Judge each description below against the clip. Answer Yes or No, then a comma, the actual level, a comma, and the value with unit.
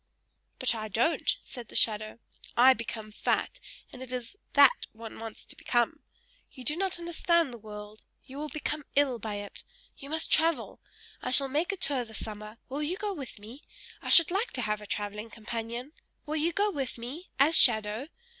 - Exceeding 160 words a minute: Yes, average, 190 wpm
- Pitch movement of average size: No, wide, 5.7 semitones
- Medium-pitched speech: No, very high, 255 Hz